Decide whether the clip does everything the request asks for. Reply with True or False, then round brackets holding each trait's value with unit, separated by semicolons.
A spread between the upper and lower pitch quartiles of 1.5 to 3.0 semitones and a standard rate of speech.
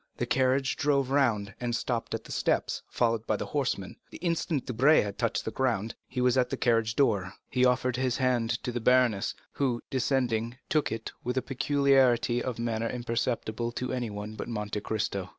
True (2.4 semitones; 185 wpm)